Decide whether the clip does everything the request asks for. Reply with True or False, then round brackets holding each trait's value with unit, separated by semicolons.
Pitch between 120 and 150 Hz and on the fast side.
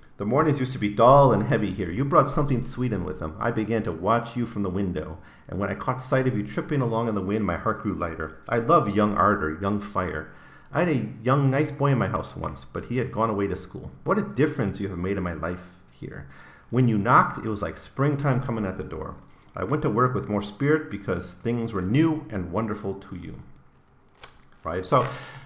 False (105 Hz; 240 wpm)